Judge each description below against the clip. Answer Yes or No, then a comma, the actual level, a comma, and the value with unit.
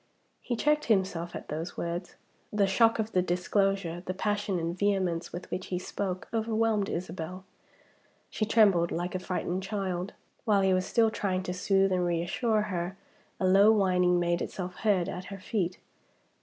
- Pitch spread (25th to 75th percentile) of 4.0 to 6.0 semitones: No, narrow, 2.5 semitones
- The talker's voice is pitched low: No, medium, 185 Hz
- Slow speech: No, average, 170 wpm